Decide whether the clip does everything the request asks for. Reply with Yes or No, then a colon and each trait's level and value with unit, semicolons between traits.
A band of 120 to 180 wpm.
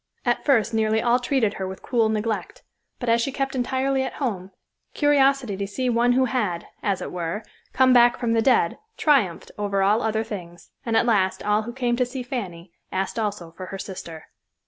No: average, 200 wpm